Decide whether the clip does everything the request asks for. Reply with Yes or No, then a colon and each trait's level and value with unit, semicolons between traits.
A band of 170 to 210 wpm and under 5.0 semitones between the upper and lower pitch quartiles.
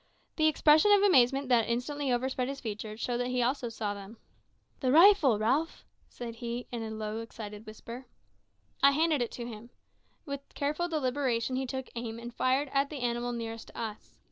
Yes: average, 185 wpm; average, 3.5 semitones